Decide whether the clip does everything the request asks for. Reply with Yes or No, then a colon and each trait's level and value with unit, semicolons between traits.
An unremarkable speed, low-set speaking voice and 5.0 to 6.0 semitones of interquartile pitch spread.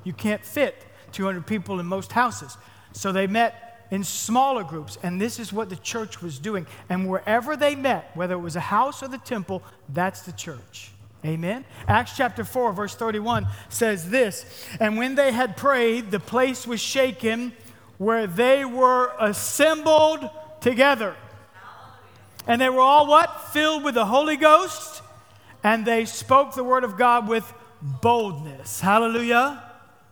No: average, 155 wpm; high, 230 Hz; wide, 5.4 semitones